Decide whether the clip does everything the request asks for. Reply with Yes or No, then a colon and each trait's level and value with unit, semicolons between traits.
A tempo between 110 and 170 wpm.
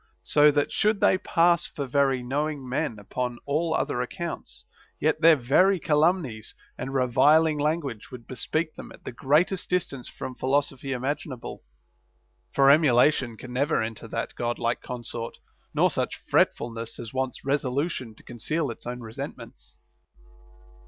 Yes: average, 150 wpm